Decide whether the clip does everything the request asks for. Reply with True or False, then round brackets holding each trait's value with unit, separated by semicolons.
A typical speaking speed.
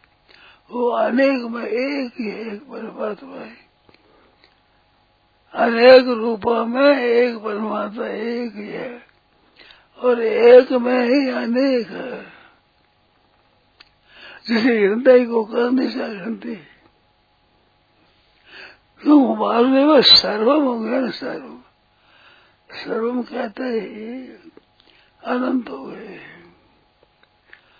False (80 wpm)